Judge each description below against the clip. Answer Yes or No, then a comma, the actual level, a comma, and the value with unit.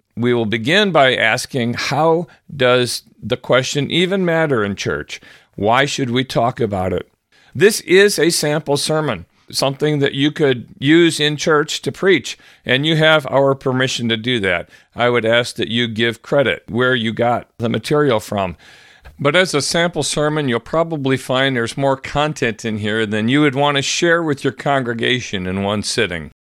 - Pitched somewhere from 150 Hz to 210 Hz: No, low, 135 Hz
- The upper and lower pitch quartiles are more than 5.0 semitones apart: No, average, 4.3 semitones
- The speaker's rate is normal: Yes, average, 180 wpm